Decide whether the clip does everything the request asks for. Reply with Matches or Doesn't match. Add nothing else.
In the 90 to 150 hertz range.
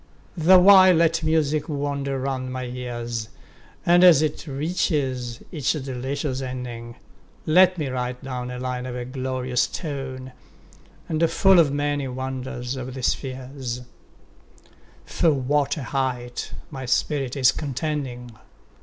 Matches